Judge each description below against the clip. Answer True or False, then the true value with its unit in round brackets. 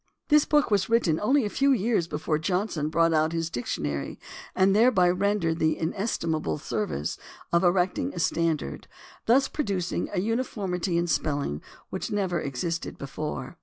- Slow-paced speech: False (155 wpm)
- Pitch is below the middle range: False (175 Hz)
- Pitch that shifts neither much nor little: True (4.6 semitones)